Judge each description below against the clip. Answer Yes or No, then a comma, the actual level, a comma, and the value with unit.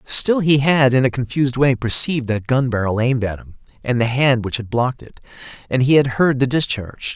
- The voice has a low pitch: Yes, low, 125 Hz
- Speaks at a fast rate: Yes, fast, 225 wpm